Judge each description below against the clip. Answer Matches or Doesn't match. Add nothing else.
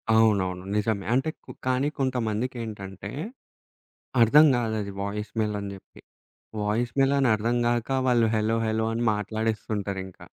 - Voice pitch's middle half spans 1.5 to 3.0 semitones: Matches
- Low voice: Matches